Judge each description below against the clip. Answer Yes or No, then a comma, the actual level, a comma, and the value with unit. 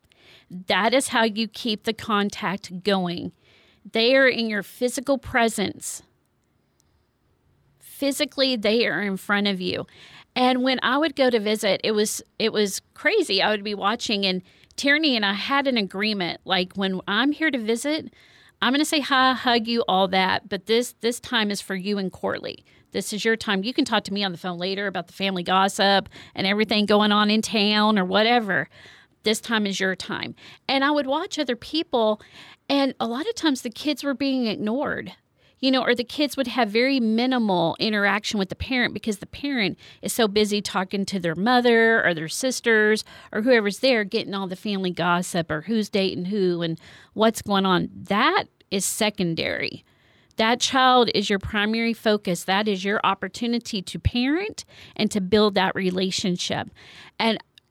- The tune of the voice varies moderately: Yes, average, 4.0 semitones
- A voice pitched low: No, high, 215 Hz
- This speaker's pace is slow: No, average, 185 wpm